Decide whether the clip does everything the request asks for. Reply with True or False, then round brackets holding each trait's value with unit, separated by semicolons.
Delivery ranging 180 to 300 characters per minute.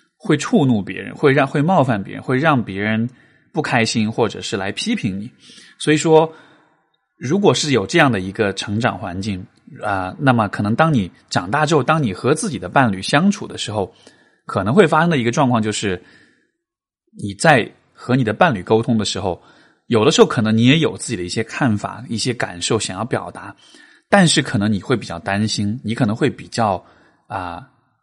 True (285 characters per minute)